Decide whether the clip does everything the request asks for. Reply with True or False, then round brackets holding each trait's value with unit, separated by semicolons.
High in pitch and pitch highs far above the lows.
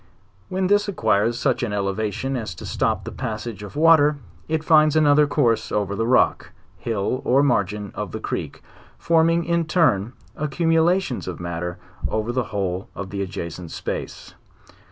False (120 Hz; 7.5 semitones)